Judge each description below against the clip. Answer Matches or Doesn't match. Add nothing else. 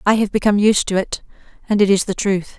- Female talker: Matches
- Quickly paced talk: Matches